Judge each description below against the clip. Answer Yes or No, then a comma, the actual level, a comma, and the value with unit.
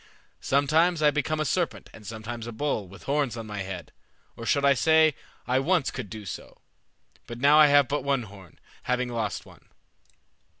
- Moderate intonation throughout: Yes, average, 4.9 semitones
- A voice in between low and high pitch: No, low, 130 Hz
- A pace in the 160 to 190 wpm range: Yes, average, 185 wpm